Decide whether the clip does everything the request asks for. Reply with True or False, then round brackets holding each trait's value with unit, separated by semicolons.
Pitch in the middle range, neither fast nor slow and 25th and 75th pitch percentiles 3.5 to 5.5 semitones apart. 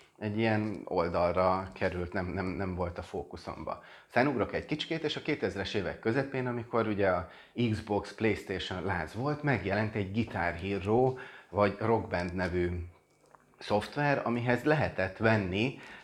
False (105 Hz; 140 wpm; 4.2 semitones)